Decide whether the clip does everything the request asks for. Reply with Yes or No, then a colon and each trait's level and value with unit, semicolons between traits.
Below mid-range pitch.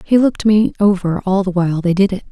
No: high, 190 Hz